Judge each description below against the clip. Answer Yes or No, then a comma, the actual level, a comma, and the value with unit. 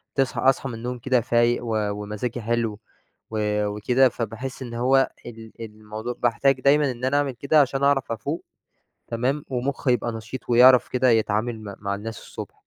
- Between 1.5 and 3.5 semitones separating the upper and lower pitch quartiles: Yes, average, 2.9 semitones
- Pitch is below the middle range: Yes, low, 120 Hz